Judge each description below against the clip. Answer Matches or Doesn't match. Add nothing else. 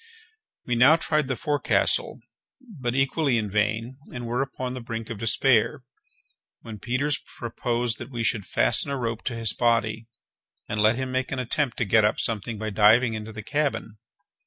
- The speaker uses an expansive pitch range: Doesn't match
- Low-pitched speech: Matches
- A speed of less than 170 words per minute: Doesn't match